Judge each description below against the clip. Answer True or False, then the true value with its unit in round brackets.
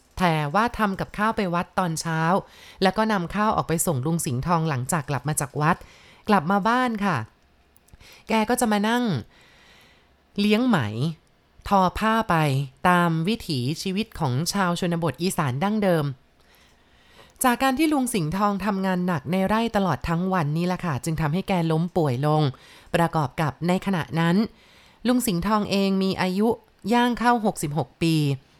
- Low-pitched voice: False (180 Hz)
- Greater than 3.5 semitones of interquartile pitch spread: True (5.2 semitones)